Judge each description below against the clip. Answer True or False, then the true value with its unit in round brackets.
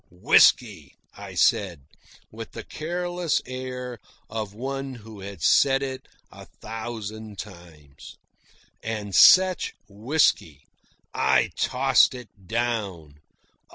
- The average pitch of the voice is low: True (110 Hz)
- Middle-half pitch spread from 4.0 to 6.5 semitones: True (4.9 semitones)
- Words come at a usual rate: False (100 wpm)